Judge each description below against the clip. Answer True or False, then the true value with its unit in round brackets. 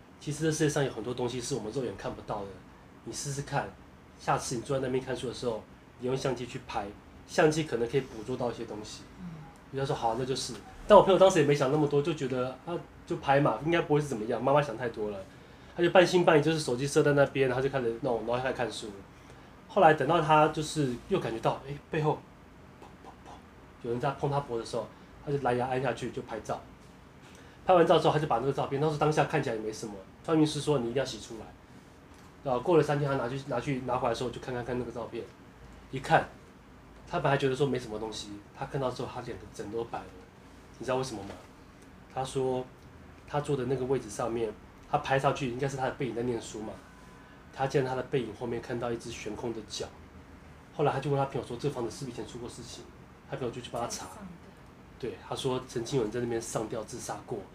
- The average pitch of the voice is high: False (130 Hz)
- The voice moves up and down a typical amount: True (3.8 semitones)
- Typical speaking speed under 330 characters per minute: False (350 characters per minute)